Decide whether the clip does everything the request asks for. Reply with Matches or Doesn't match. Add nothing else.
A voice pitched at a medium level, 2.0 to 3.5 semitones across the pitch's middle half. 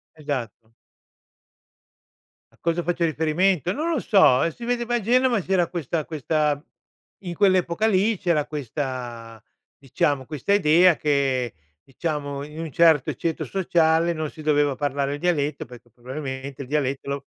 Doesn't match